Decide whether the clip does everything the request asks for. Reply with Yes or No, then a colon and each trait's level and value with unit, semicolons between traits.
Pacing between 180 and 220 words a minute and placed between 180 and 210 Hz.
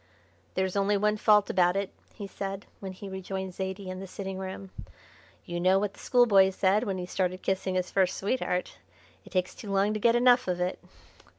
Yes: average, 200 wpm; high, 190 Hz